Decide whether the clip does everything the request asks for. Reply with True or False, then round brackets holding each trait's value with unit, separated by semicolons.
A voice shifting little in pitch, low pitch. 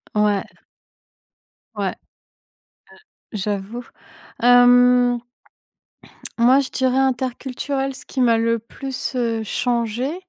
False (2.2 semitones; 245 Hz)